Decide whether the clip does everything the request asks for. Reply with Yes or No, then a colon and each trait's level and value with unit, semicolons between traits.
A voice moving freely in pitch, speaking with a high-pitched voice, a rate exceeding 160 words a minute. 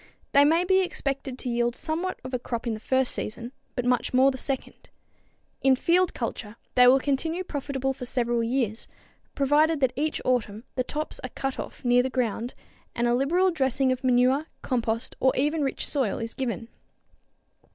No: average, 2.8 semitones; very high, 260 Hz; average, 180 wpm